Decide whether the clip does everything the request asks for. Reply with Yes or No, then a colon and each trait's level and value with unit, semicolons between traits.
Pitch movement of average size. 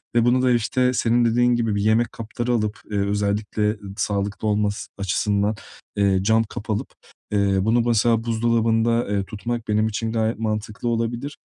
No: narrow, 2.2 semitones